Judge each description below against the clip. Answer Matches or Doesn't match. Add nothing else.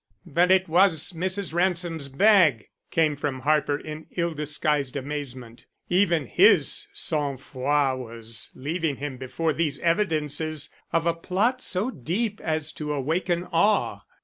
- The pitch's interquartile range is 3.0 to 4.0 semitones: Matches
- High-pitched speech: Doesn't match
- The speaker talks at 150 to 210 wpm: Doesn't match